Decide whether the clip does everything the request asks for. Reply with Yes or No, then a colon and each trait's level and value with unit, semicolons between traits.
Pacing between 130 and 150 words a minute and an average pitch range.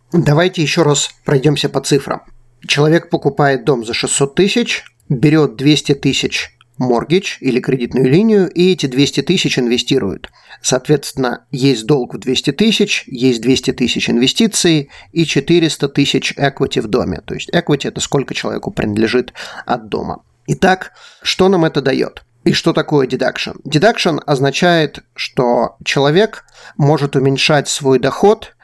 Yes: average, 140 wpm; average, 4.0 semitones